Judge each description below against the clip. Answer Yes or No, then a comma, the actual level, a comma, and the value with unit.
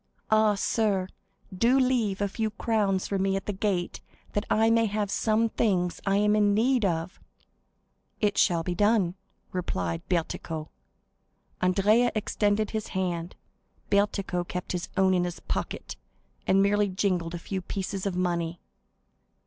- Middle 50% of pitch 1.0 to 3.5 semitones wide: Yes, average, 2.9 semitones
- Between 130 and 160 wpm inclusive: Yes, average, 150 wpm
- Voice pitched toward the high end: Yes, high, 195 Hz